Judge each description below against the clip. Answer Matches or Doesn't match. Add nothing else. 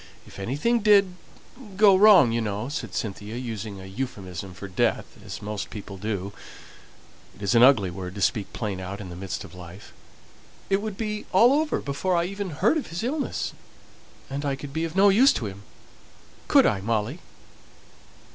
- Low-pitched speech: Matches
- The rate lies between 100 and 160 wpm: Doesn't match